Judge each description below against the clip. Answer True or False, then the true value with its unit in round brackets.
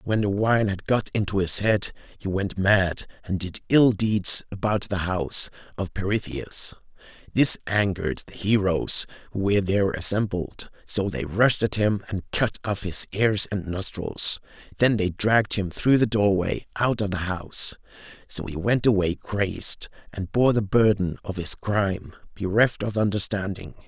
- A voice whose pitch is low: True (100 Hz)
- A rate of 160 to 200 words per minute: True (165 wpm)